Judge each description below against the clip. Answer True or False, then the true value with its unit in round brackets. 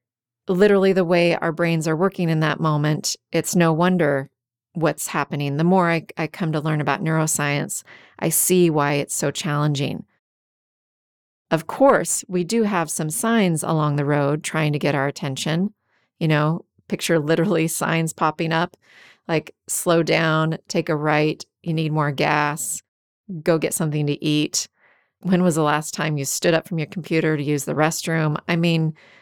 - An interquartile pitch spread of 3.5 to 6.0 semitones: False (2.4 semitones)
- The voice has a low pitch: False (160 Hz)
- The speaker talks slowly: False (175 wpm)